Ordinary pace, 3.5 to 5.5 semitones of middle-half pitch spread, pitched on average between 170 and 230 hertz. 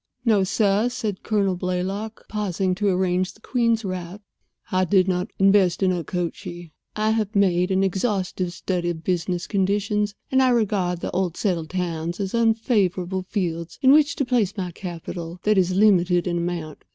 No: average, 160 wpm; average, 2.8 semitones; high, 190 Hz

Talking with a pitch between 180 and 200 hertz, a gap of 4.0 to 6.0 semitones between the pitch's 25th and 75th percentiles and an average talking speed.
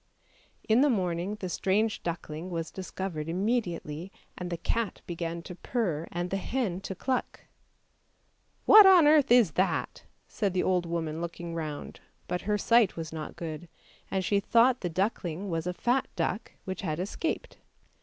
Yes: medium, 185 Hz; average, 4.4 semitones; average, 175 wpm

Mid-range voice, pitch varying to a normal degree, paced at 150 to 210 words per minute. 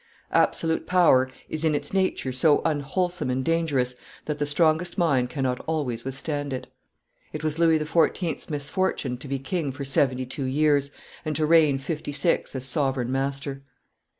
Yes: medium, 145 Hz; average, 3.3 semitones; average, 160 wpm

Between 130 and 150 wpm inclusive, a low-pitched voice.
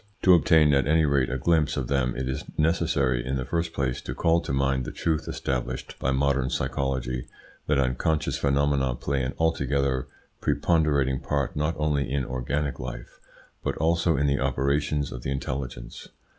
No: average, 170 wpm; very low, 70 Hz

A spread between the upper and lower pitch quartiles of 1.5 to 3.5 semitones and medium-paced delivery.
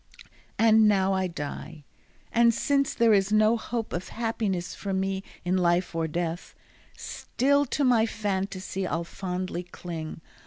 No: average, 4.0 semitones; average, 145 wpm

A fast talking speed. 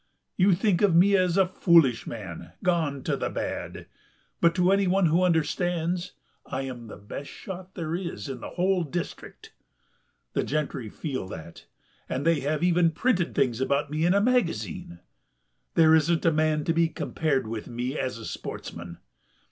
No: average, 170 wpm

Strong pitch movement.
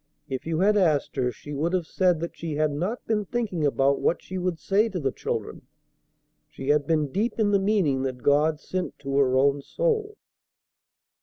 Yes: wide, 5.7 semitones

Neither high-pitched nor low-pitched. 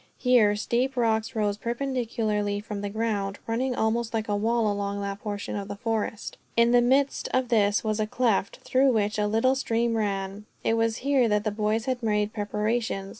No: high, 220 Hz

